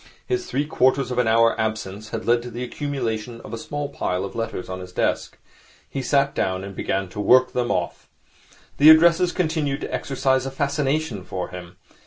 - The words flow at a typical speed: Yes, average, 195 wpm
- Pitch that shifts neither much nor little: Yes, average, 4.9 semitones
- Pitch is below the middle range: Yes, low, 125 Hz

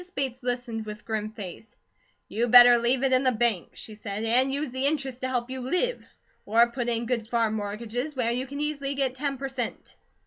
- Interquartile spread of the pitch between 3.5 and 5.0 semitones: No, average, 2.7 semitones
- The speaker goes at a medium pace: No, fast, 215 wpm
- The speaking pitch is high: Yes, high, 245 Hz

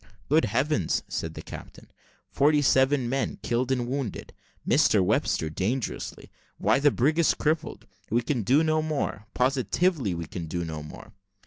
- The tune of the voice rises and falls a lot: Yes, wide, 5.8 semitones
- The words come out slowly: No, average, 155 wpm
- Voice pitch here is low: Yes, low, 130 Hz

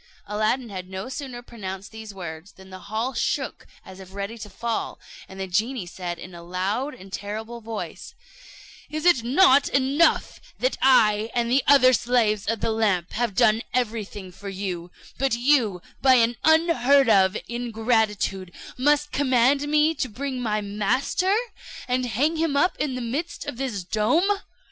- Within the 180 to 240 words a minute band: No, average, 165 wpm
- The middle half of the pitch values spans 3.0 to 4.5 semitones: No, average, 5.0 semitones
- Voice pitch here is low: No, high, 230 Hz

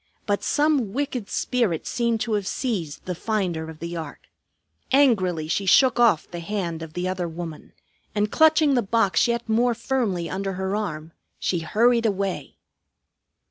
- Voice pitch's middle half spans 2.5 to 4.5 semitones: No, wide, 5.4 semitones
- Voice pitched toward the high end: Yes, high, 200 Hz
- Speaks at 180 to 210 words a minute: No, average, 160 wpm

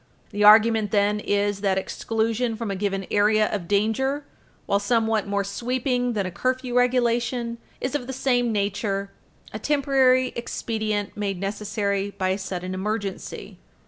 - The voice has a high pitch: Yes, high, 215 Hz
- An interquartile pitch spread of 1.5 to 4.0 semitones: Yes, average, 3.3 semitones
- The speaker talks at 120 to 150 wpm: Yes, average, 145 wpm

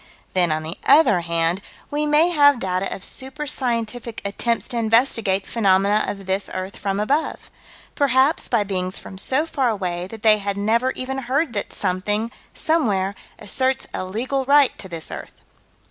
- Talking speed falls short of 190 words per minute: Yes, average, 165 wpm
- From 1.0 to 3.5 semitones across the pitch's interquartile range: No, wide, 5.6 semitones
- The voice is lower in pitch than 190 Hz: No, high, 215 Hz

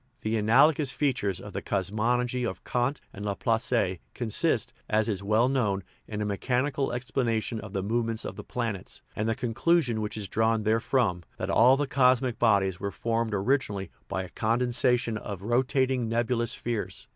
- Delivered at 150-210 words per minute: Yes, average, 175 wpm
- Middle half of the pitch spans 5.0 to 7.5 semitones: No, average, 3.2 semitones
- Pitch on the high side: No, low, 115 Hz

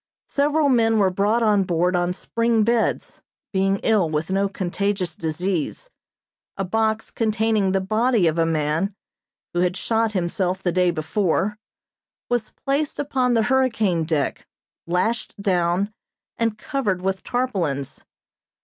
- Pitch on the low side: No, high, 195 Hz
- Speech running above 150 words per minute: No, slow, 135 wpm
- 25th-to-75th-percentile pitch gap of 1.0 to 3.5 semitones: No, average, 4.1 semitones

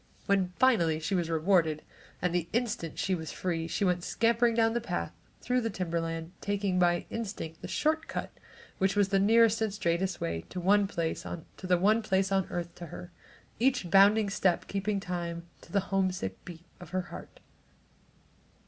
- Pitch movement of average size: Yes, average, 3.3 semitones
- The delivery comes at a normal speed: Yes, average, 170 wpm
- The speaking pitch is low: No, medium, 185 Hz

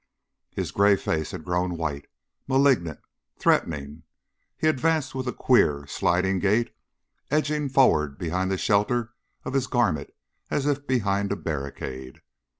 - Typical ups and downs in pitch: No, wide, 8.7 semitones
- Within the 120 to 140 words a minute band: Yes, slow, 135 wpm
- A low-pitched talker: Yes, low, 100 Hz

